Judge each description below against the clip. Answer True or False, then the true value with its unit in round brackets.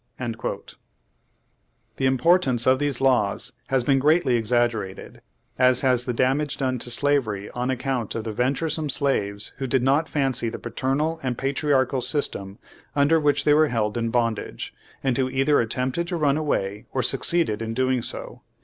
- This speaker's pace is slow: False (165 wpm)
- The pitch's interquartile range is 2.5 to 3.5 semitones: True (3.1 semitones)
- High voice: False (130 Hz)